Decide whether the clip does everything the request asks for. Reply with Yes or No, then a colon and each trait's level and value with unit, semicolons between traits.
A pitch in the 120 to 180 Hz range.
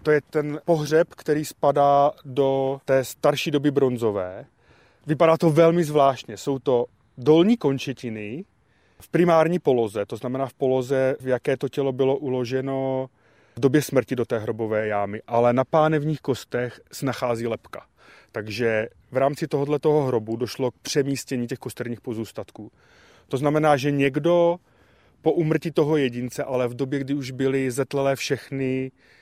Yes: low, 135 Hz